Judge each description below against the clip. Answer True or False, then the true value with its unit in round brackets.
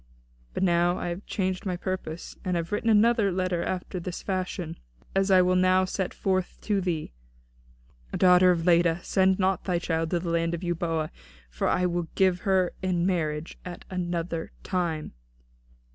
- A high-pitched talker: False (180 Hz)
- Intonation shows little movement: True (1.6 semitones)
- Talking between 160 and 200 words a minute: True (170 wpm)